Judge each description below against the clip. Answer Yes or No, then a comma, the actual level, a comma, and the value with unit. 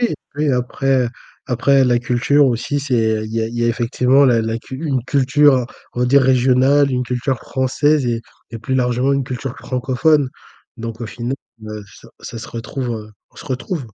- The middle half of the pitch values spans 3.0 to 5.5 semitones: No, narrow, 2.5 semitones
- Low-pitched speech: Yes, low, 125 Hz